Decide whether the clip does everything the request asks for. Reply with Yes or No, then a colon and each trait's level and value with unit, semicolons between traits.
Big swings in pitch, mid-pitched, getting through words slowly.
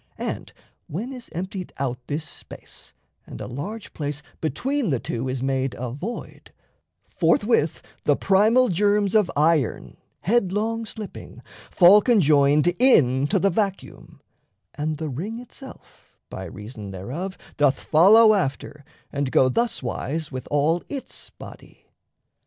Yes: wide, 7.1 semitones; medium, 165 Hz; slow, 130 wpm